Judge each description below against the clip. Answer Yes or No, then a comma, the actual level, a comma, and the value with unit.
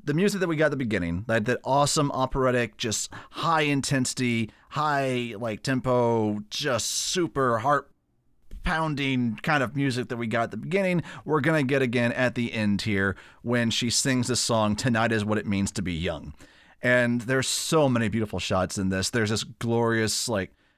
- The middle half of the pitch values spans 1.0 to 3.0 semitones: No, average, 4.1 semitones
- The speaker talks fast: No, average, 190 wpm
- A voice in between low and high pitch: No, low, 120 Hz